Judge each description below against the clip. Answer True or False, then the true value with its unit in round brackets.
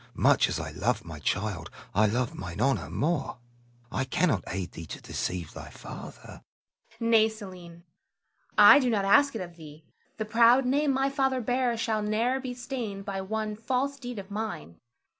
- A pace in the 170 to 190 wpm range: True (180 wpm)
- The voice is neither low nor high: False (210 Hz)